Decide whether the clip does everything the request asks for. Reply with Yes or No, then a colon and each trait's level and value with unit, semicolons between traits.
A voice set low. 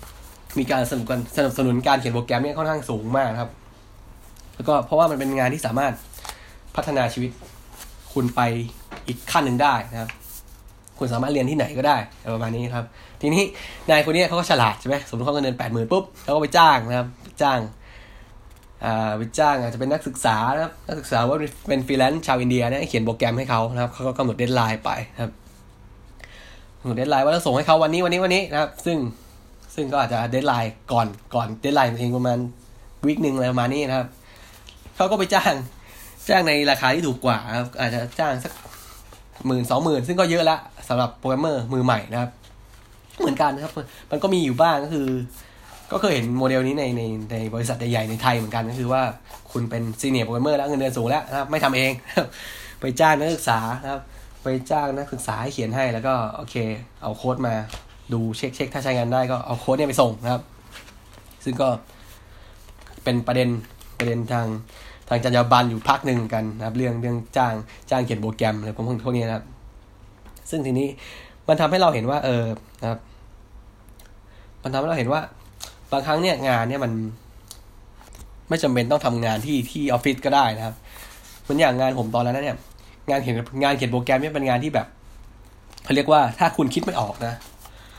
Yes: low, 120 Hz